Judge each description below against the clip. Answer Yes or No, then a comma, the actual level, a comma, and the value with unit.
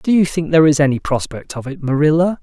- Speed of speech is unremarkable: No, fast, 250 wpm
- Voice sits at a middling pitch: Yes, medium, 150 Hz